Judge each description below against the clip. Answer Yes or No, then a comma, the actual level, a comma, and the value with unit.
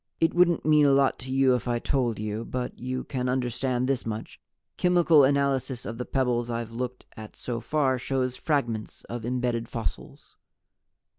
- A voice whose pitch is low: Yes, low, 125 Hz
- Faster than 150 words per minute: Yes, average, 170 wpm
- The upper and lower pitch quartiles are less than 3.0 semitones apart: Yes, narrow, 2.4 semitones